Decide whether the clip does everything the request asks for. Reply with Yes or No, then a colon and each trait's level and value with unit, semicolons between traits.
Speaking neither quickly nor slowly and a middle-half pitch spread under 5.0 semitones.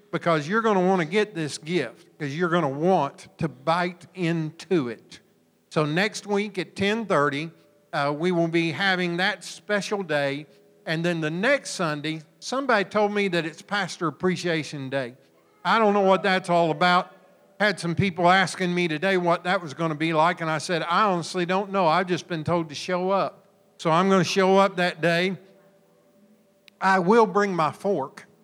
Yes: average, 190 wpm; average, 3.1 semitones